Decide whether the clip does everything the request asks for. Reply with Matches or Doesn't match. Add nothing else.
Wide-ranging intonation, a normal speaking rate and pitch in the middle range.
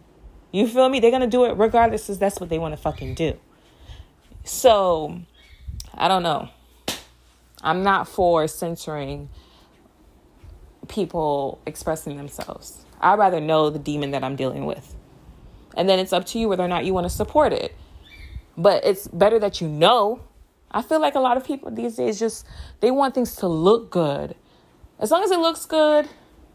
Matches